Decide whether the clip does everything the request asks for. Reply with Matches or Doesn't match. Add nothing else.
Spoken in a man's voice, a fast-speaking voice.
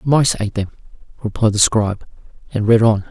Doesn't match